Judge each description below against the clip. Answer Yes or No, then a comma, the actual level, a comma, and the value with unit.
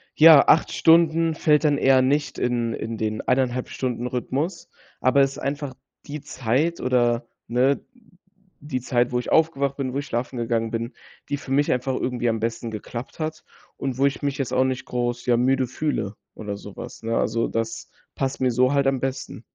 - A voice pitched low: Yes, low, 130 Hz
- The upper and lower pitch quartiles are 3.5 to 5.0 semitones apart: No, average, 2.8 semitones